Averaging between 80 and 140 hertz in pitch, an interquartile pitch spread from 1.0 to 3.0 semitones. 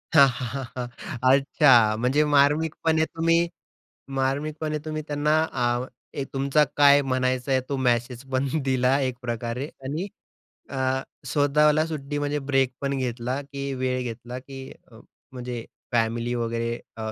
Yes: low, 135 Hz; average, 2.7 semitones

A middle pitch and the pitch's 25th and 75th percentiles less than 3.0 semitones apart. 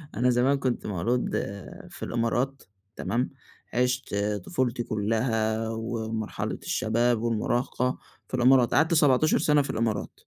No: low, 120 Hz; narrow, 2.4 semitones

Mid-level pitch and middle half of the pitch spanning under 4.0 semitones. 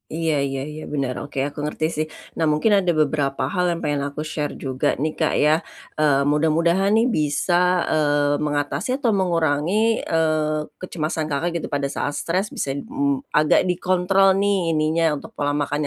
Yes: medium, 155 Hz; average, 3.6 semitones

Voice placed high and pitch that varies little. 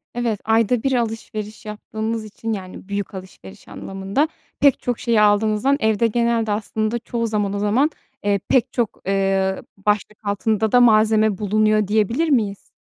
Yes: high, 215 Hz; narrow, 2.1 semitones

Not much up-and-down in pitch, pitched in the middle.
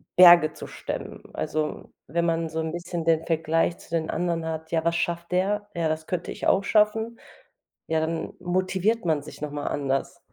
Yes: narrow, 2.0 semitones; medium, 165 Hz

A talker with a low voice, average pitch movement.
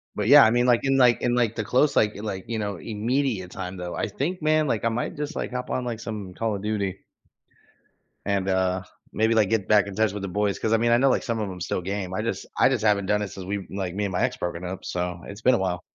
Yes: low, 105 Hz; average, 3.6 semitones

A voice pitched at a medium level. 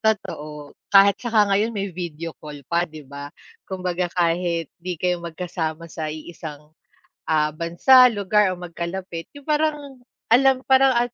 Yes: medium, 180 Hz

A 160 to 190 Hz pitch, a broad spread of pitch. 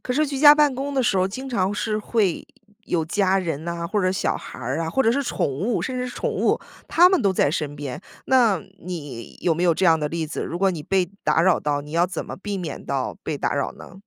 Yes: medium, 185 Hz; wide, 6.5 semitones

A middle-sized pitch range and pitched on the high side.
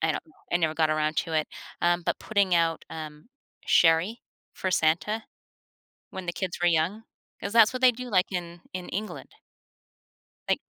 No: average, 4.0 semitones; medium, 175 Hz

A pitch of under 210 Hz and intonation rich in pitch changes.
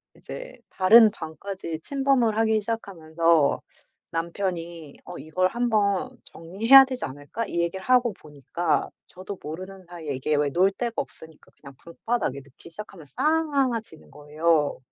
Yes: medium, 185 Hz; wide, 6.2 semitones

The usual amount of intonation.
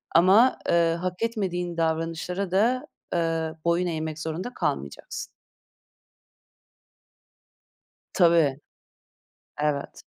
No: narrow, 2.3 semitones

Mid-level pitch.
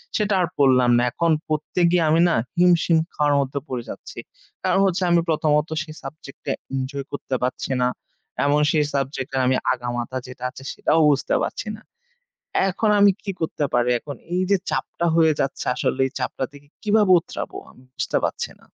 Yes: medium, 145 Hz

